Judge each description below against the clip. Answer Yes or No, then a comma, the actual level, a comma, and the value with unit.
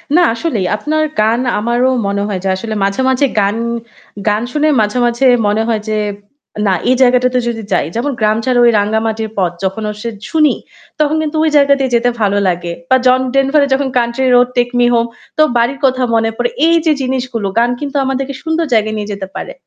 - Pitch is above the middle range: Yes, high, 240 Hz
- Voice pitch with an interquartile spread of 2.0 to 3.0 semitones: No, average, 3.9 semitones